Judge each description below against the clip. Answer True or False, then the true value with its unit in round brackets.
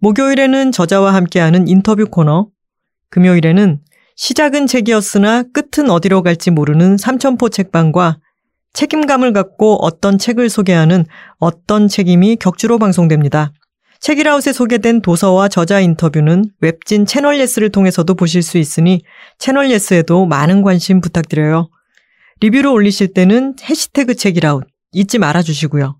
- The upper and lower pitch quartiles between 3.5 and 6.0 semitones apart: True (5.3 semitones)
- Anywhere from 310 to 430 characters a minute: True (335 characters per minute)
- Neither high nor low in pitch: False (195 Hz)